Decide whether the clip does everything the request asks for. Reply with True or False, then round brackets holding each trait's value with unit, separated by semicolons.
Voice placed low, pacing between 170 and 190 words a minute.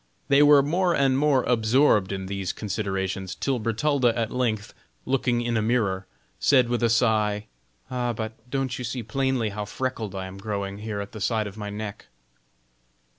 True (115 Hz; 175 wpm)